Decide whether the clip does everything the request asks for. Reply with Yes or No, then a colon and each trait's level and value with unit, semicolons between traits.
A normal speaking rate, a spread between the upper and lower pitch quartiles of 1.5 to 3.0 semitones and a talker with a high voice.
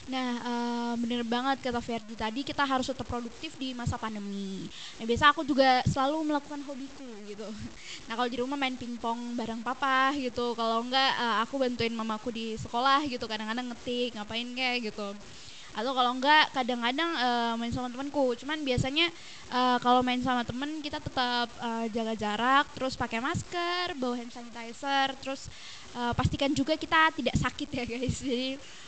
No: fast, 170 wpm; narrow, 2.5 semitones; very high, 250 Hz